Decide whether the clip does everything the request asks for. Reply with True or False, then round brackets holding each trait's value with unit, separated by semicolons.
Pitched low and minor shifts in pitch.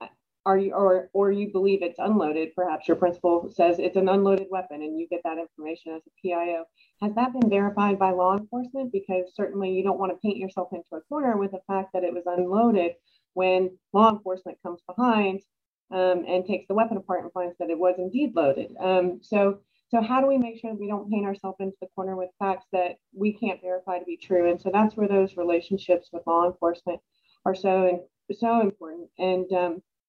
False (185 Hz; 2.1 semitones)